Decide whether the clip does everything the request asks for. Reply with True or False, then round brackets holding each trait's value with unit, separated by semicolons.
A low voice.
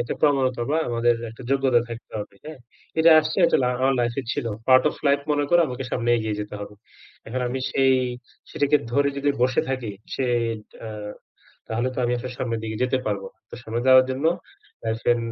True (125 Hz)